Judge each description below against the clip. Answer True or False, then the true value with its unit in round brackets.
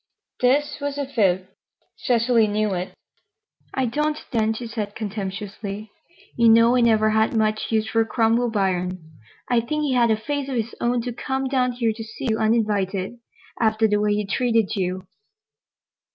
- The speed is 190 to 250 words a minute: False (170 wpm)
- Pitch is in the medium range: False (225 Hz)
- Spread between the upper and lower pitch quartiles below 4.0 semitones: True (2.7 semitones)